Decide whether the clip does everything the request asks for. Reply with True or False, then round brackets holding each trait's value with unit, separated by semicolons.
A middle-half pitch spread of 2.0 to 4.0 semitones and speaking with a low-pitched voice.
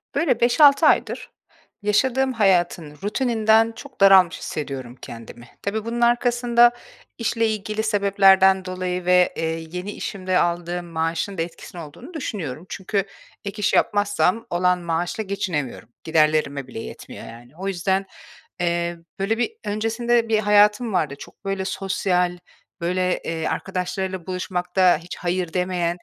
False (3.7 semitones; 190 Hz)